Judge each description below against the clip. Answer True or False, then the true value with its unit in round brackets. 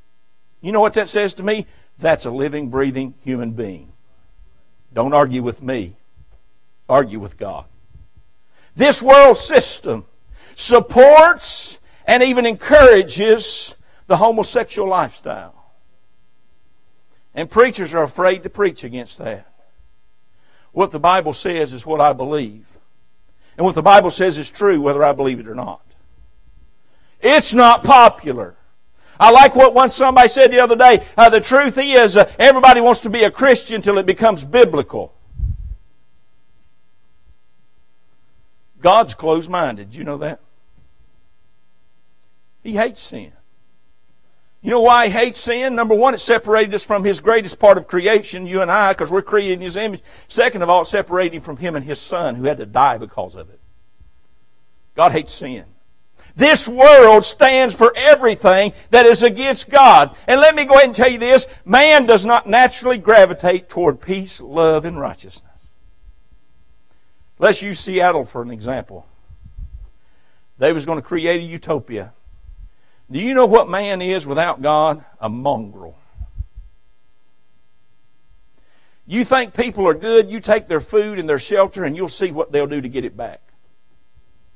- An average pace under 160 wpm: True (150 wpm)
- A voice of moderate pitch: True (175 Hz)